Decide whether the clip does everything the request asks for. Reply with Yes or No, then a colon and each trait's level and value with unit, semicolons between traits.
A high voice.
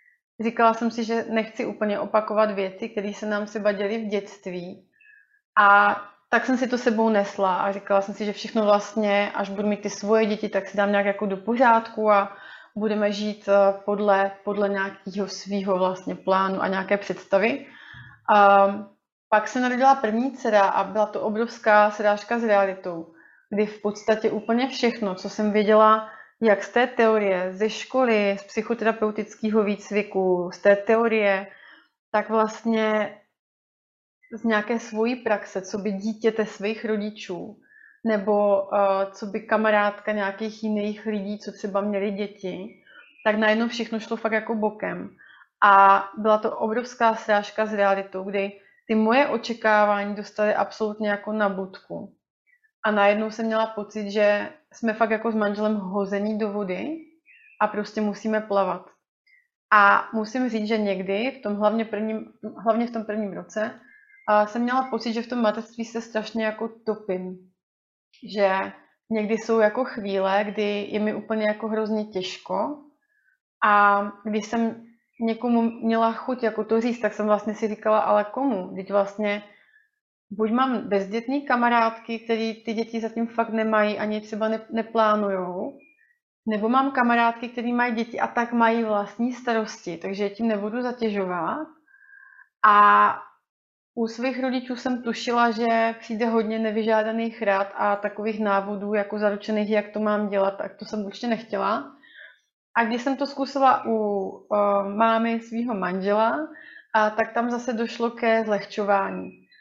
Yes: high, 215 Hz